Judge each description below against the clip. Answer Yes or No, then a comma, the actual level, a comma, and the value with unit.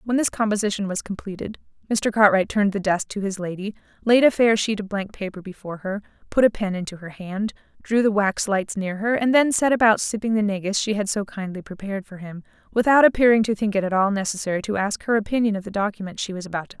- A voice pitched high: Yes, high, 205 Hz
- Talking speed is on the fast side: Yes, fast, 245 wpm